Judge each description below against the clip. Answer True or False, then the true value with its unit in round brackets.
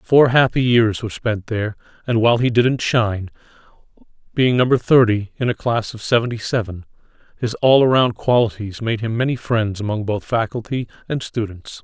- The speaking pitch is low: True (115 Hz)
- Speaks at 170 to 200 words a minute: False (160 wpm)